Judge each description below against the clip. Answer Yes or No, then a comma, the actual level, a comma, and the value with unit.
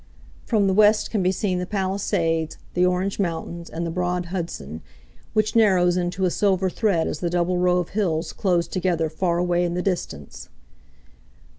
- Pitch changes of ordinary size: No, narrow, 1.9 semitones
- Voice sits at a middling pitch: Yes, medium, 180 Hz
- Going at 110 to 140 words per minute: No, average, 175 wpm